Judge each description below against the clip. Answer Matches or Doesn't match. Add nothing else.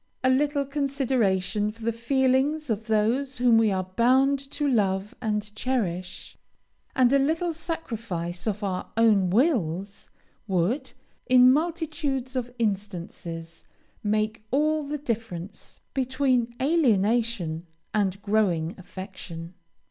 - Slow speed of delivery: Matches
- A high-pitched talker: Matches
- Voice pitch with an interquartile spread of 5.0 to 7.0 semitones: Matches